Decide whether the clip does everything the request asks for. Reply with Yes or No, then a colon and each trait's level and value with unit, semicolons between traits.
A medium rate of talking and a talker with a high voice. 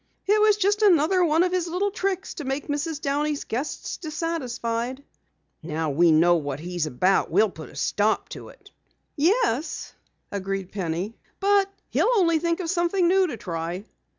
Yes: average, 165 wpm; very high, 290 Hz